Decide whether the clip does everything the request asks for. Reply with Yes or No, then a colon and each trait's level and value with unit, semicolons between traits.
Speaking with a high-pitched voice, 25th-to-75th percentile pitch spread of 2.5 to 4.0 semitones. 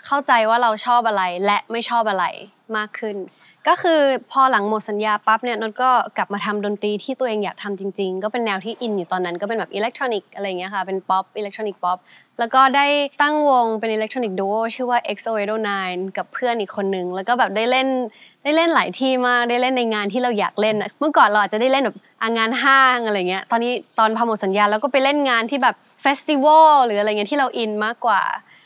Yes: high, 225 Hz; average, 3.7 semitones